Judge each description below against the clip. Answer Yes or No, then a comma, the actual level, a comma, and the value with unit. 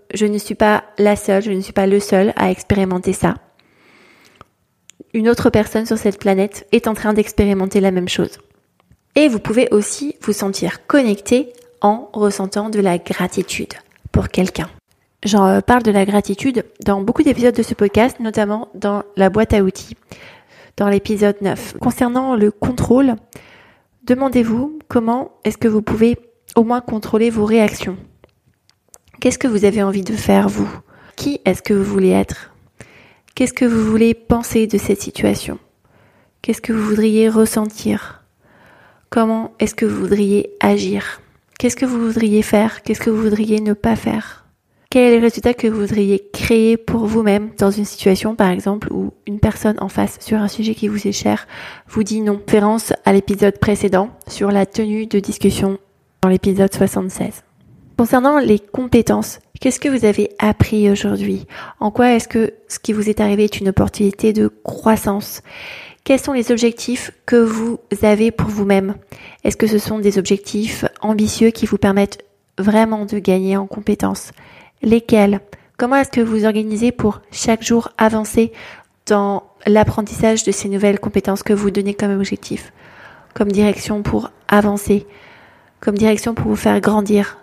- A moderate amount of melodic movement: No, narrow, 2.2 semitones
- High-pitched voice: Yes, high, 210 Hz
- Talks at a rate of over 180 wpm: No, average, 165 wpm